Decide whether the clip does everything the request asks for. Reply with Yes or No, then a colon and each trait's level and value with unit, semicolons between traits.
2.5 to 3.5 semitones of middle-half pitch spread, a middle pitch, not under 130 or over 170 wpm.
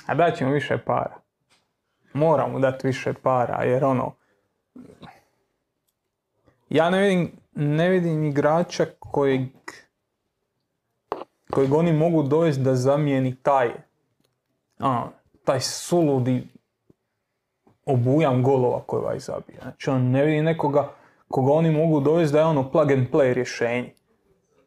No: average, 3.2 semitones; medium, 145 Hz; average, 120 wpm